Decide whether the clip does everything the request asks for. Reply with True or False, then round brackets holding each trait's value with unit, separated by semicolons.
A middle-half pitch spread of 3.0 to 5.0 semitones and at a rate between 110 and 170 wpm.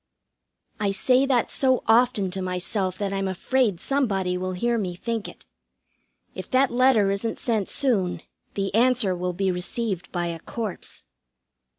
True (4.6 semitones; 155 wpm)